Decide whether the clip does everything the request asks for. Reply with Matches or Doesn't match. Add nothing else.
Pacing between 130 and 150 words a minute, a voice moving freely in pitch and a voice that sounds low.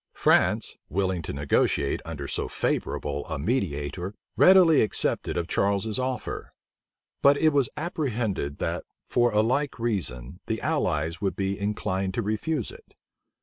Matches